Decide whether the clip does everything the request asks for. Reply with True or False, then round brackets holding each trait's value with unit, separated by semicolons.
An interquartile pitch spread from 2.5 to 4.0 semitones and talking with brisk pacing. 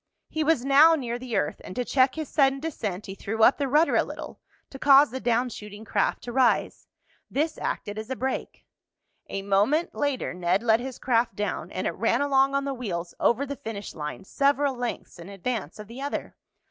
False (4.8 semitones; 210 wpm)